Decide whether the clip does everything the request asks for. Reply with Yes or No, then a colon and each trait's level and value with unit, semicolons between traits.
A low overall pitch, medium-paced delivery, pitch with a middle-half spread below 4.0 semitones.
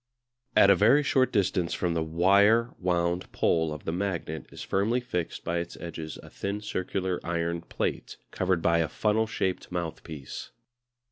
Yes: very low, 90 Hz; average, 160 wpm; average, 3.1 semitones